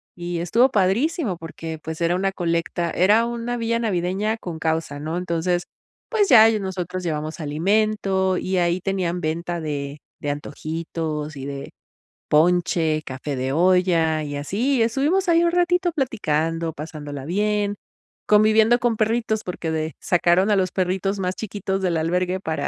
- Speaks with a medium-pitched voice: Yes, medium, 180 Hz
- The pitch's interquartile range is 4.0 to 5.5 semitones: Yes, average, 4.9 semitones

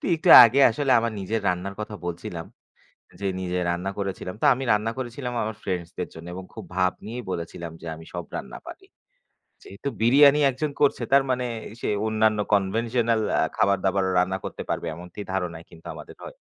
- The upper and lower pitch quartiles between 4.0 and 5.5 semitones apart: Yes, average, 4.5 semitones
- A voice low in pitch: Yes, low, 100 Hz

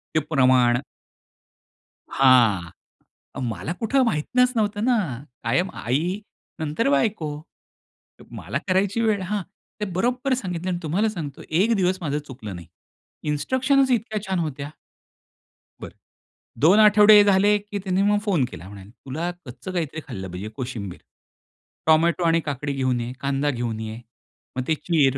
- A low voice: No, medium, 160 Hz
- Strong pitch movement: Yes, wide, 7.9 semitones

